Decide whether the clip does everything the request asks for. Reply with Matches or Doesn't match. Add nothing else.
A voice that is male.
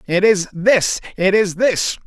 Matches